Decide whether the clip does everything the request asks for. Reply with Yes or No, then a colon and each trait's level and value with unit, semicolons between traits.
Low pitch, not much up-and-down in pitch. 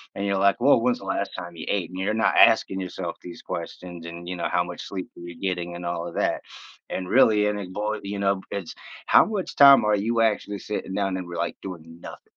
No: very low, 95 Hz; average, 3.1 semitones